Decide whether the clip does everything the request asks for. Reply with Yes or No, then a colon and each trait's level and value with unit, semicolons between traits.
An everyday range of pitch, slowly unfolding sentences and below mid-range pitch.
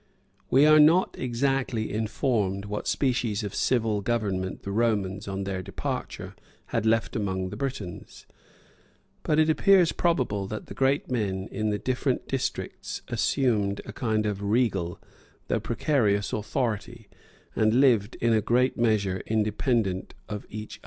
No: average, 4.0 semitones; average, 145 wpm; low, 110 Hz